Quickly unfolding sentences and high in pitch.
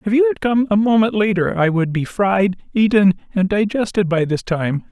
Yes: fast, 210 wpm; high, 195 Hz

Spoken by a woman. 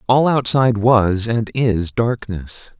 No: male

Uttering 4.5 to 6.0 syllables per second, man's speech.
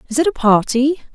No: 5.9 syllables/s; female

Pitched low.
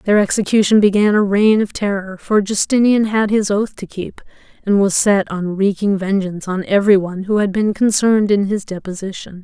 No: high, 200 Hz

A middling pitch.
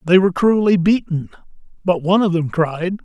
Yes: medium, 180 Hz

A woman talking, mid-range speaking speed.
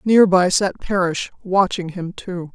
Yes: female; average, 165 wpm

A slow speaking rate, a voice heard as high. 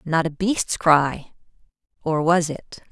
No: slow, 125 wpm; medium, 165 Hz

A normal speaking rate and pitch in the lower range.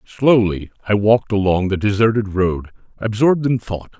Yes: average, 150 wpm; low, 105 Hz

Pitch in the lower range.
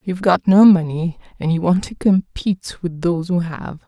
No: medium, 175 Hz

